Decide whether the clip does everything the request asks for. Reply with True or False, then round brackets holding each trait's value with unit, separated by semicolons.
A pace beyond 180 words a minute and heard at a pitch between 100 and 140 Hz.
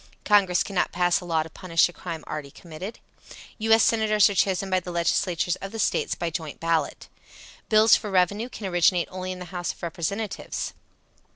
False (190 wpm; 180 Hz)